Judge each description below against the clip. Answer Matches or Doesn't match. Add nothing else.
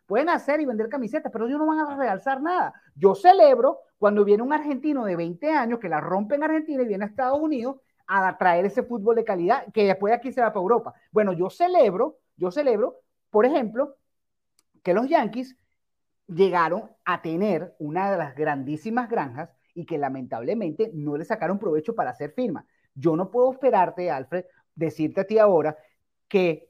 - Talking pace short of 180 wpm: Doesn't match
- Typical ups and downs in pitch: Doesn't match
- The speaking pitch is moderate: Doesn't match